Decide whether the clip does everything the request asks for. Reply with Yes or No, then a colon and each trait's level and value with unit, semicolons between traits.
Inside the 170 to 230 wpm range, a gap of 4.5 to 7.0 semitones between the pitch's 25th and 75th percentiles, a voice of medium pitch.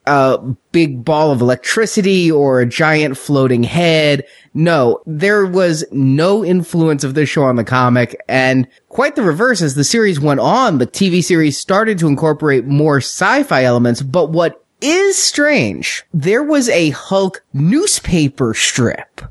No: average, 150 wpm; average, 5.2 semitones; medium, 155 Hz